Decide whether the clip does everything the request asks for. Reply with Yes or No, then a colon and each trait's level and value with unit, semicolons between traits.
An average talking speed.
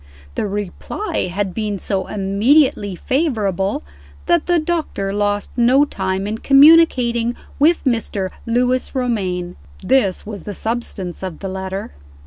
No: slow, 125 wpm